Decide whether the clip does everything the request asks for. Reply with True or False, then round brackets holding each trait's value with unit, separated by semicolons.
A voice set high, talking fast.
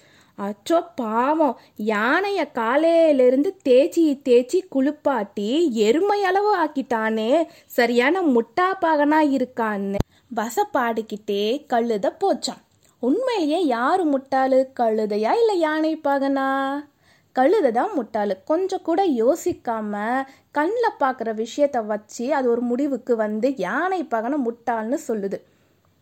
False (270 Hz; 95 wpm)